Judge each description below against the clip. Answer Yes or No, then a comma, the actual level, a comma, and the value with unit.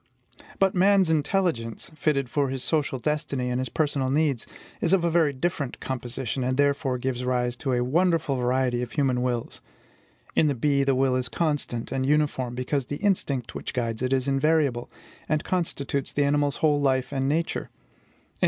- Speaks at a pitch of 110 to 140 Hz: Yes, low, 135 Hz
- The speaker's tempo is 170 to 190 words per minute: Yes, average, 175 wpm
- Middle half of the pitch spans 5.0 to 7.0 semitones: No, average, 3.2 semitones